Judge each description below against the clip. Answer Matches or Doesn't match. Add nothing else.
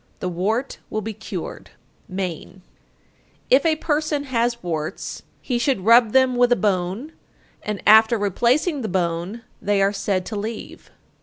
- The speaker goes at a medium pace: Matches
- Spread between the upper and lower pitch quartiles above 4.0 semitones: Matches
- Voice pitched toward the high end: Matches